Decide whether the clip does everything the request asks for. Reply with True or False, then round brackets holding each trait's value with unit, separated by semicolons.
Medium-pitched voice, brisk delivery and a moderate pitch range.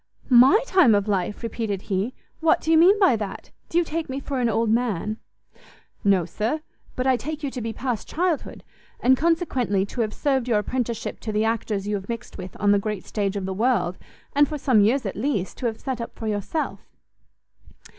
False (230 Hz; 210 wpm; 4.9 semitones)